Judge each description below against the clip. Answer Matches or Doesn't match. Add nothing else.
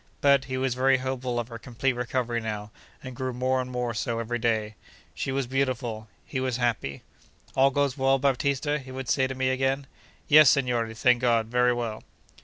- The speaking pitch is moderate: Doesn't match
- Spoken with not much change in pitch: Matches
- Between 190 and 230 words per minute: Matches